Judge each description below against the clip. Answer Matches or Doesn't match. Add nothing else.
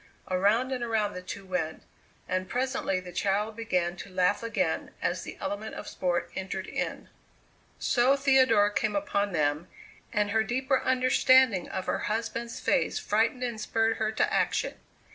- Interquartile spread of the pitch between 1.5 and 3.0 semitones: Doesn't match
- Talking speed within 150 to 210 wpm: Matches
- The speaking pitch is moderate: Doesn't match